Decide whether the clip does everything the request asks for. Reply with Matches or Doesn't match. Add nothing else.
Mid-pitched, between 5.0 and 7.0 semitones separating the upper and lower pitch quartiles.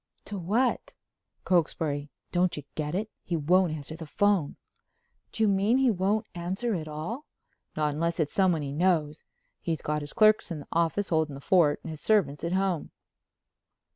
Doesn't match